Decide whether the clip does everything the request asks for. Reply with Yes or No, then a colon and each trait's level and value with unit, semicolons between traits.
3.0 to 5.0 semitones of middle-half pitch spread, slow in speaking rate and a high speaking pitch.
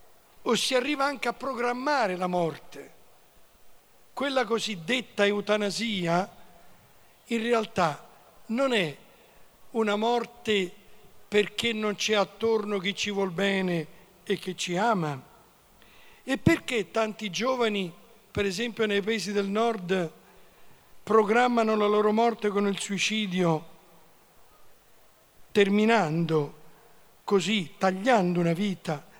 Yes: average, 3.7 semitones; slow, 105 wpm; high, 205 Hz